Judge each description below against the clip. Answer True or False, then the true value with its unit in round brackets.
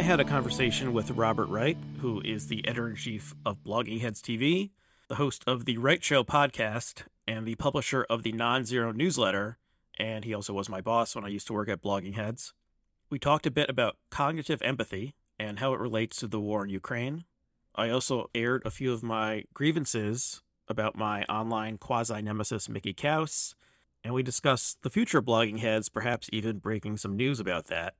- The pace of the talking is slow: False (190 wpm)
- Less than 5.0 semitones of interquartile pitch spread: True (3.3 semitones)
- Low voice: True (115 Hz)